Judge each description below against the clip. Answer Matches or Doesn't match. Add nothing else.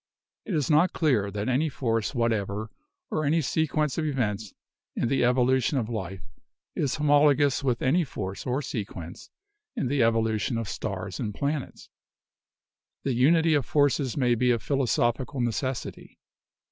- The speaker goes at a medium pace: Matches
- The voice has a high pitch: Doesn't match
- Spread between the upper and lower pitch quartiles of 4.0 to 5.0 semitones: Matches